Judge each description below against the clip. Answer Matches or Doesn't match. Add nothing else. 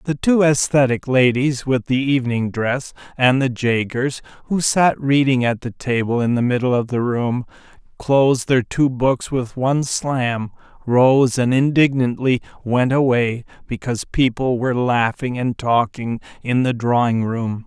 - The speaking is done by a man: Matches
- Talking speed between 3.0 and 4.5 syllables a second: Matches